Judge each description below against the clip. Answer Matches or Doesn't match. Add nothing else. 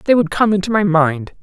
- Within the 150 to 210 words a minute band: Doesn't match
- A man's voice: Doesn't match